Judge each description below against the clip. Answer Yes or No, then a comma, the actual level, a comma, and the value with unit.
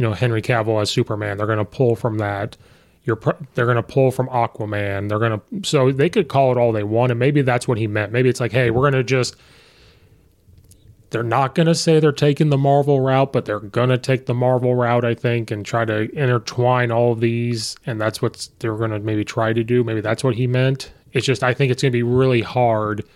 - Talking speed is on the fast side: Yes, fast, 250 wpm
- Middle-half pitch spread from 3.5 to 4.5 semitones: No, average, 2.9 semitones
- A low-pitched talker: Yes, low, 120 Hz